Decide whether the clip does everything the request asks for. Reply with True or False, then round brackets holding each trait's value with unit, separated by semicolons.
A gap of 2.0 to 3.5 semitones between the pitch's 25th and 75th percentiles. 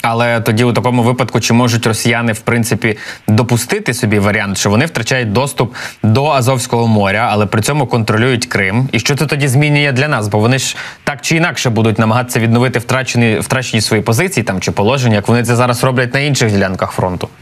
True (3.0 semitones)